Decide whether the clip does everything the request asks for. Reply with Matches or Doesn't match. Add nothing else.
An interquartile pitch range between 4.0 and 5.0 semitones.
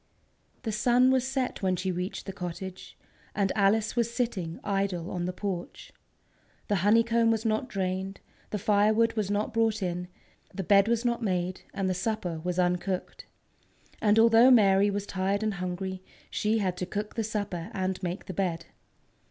Doesn't match